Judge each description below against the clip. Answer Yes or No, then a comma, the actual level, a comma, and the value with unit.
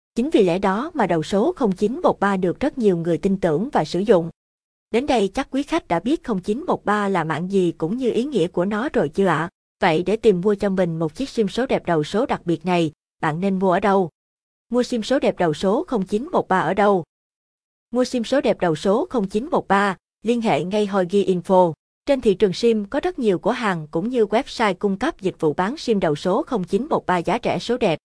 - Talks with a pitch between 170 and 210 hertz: Yes, high, 200 Hz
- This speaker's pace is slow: No, average, 225 wpm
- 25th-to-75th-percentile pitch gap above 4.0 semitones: Yes, average, 4.5 semitones